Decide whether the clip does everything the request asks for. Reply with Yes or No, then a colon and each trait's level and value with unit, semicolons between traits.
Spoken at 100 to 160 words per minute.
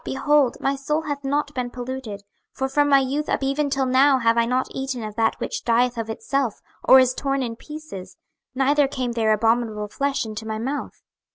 No: average, 200 wpm